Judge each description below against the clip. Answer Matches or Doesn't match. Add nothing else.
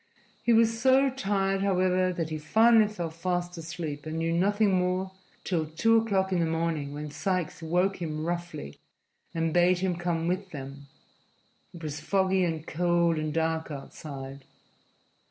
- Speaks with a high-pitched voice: Doesn't match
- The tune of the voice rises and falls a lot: Doesn't match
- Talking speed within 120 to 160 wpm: Matches